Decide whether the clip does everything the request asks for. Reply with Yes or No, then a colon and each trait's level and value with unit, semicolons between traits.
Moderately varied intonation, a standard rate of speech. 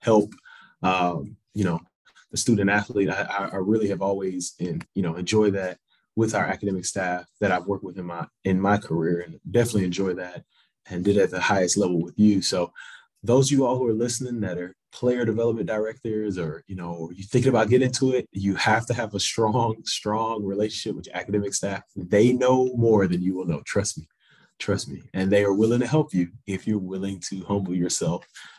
No: average, 3.4 semitones; fast, 210 wpm